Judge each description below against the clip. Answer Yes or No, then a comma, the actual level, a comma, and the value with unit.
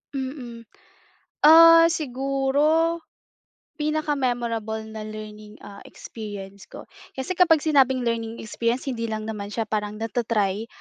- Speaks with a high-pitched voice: Yes, high, 235 Hz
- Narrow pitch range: No, average, 4.8 semitones